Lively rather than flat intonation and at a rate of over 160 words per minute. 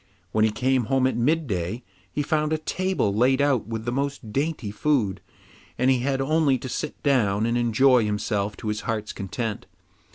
No: average, 4.4 semitones; average, 185 wpm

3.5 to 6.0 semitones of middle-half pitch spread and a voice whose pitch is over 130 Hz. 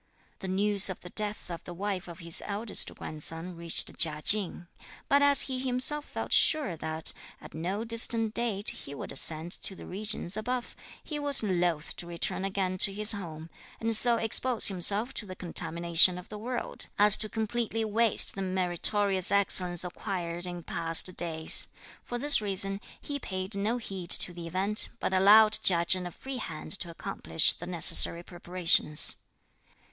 Yes: average, 3.9 semitones; high, 190 Hz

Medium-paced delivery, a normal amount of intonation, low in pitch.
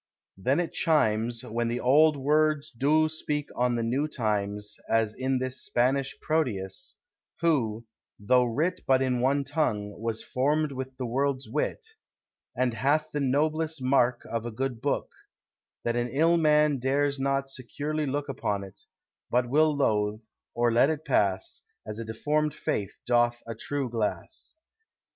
Yes: average, 155 wpm; average, 4.1 semitones; low, 130 Hz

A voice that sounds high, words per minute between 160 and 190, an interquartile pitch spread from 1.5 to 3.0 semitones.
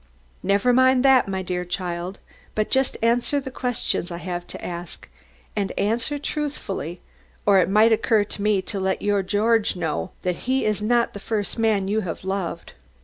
No: high, 205 Hz; average, 180 wpm; average, 4.0 semitones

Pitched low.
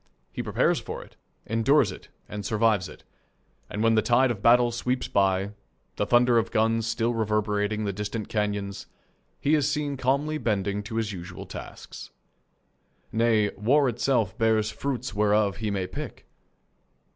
Yes: low, 110 Hz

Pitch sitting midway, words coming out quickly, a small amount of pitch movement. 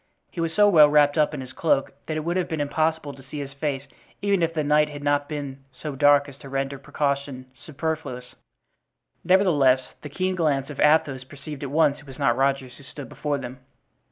Yes: medium, 145 Hz; fast, 215 wpm; narrow, 2.3 semitones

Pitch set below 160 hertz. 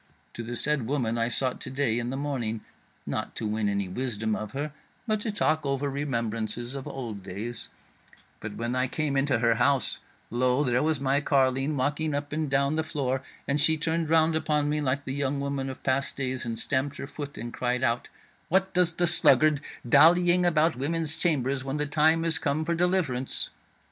Yes: medium, 140 Hz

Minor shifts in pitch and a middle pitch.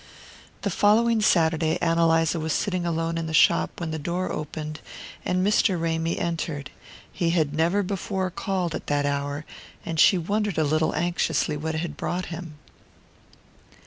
Yes: narrow, 2.3 semitones; medium, 165 Hz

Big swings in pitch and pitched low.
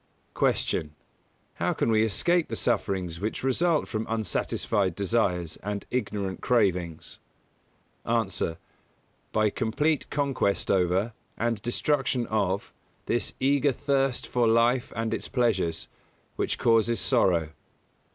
No: average, 4.4 semitones; low, 115 Hz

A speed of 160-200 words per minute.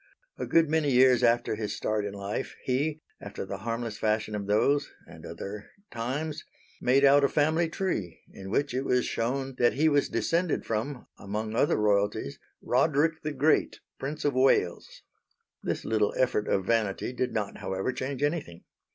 Yes: average, 170 wpm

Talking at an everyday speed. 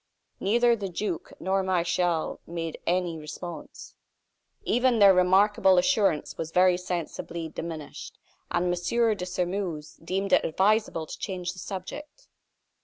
No: slow, 125 wpm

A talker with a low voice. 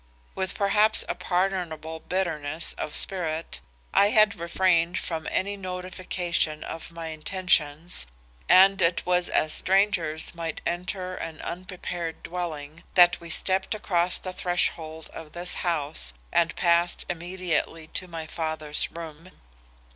No: medium, 175 Hz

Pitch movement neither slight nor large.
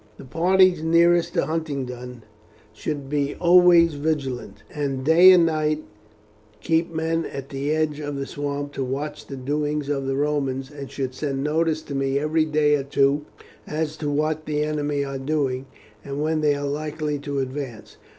No: narrow, 2.2 semitones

